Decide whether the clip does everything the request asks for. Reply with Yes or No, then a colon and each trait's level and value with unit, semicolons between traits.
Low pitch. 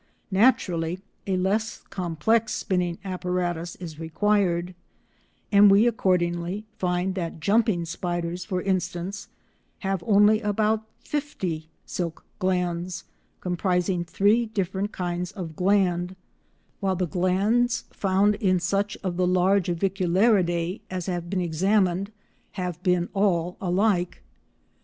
No: medium, 185 Hz